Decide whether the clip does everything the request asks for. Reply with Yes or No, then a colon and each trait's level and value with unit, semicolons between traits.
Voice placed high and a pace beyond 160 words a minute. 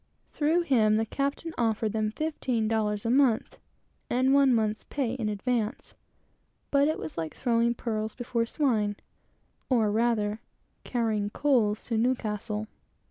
No: high, 230 Hz; slow, 135 wpm